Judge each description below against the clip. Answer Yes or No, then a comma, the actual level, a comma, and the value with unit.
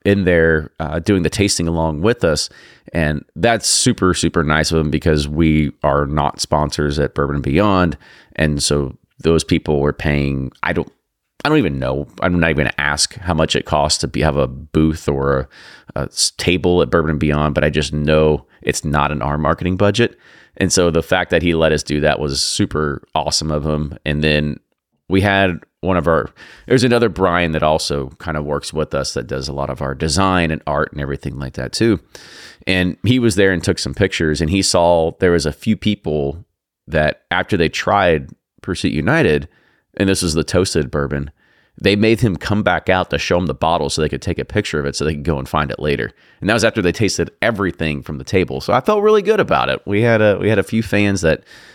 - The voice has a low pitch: Yes, very low, 80 Hz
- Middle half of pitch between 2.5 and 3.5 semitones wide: No, average, 4.2 semitones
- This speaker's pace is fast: Yes, fast, 230 wpm